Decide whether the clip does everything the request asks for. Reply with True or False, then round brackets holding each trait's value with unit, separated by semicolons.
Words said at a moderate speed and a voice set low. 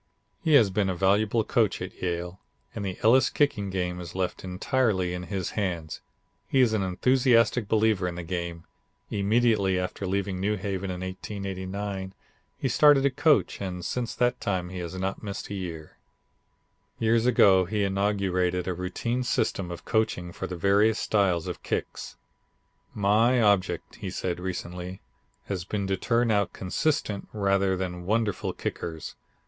True (160 wpm; 95 Hz)